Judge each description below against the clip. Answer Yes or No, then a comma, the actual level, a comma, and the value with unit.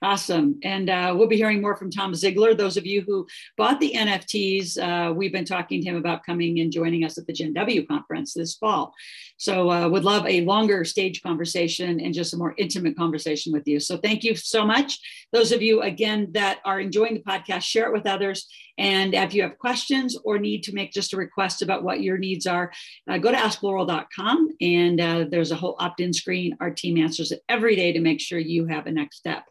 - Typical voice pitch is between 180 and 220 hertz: Yes, high, 190 Hz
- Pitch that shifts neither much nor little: Yes, average, 3.5 semitones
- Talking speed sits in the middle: No, fast, 230 wpm